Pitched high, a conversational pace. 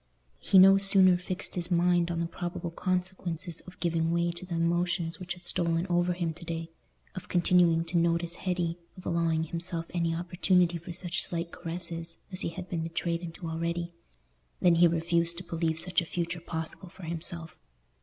No: medium, 170 Hz; average, 175 wpm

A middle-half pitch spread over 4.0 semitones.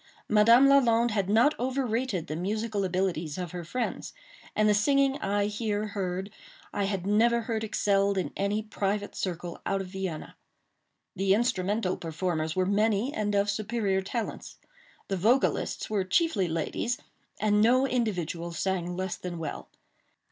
No: average, 3.4 semitones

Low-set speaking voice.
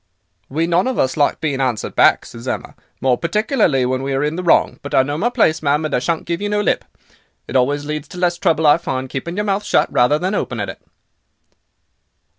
No: medium, 155 Hz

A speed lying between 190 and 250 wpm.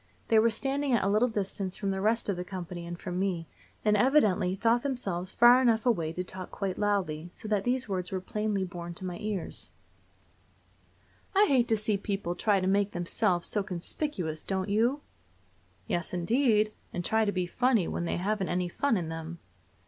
Yes: average, 195 wpm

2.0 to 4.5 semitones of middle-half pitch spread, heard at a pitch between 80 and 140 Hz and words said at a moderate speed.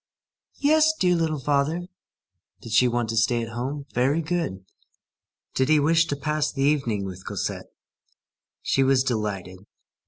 No: average, 5.0 semitones; low, 135 Hz; average, 150 wpm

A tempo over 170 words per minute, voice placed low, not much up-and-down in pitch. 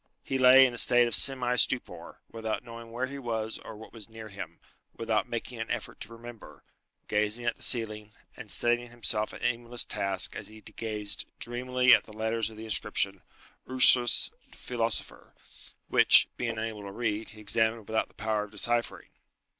Yes: average, 180 wpm; low, 115 Hz; narrow, 2.0 semitones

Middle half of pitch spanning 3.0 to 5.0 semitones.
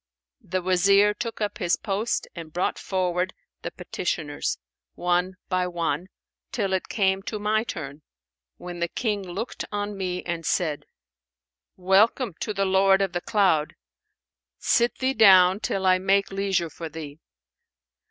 No: narrow, 2.4 semitones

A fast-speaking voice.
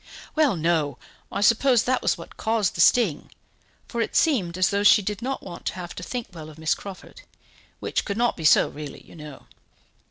Yes: fast, 210 wpm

